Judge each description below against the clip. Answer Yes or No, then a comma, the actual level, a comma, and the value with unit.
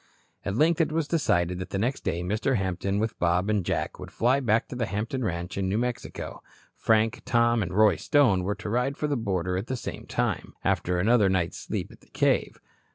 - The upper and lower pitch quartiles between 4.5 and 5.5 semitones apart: Yes, average, 4.9 semitones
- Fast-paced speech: Yes, fast, 220 wpm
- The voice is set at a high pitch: No, low, 110 Hz